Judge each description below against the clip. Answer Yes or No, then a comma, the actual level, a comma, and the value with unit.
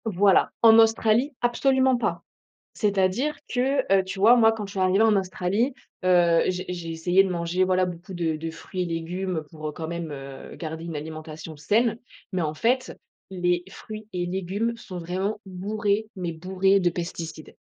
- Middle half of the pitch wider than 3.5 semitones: Yes, average, 4.1 semitones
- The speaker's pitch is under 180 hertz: No, medium, 185 Hz